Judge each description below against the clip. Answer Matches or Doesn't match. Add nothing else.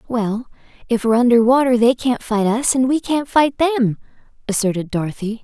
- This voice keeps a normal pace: Matches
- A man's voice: Doesn't match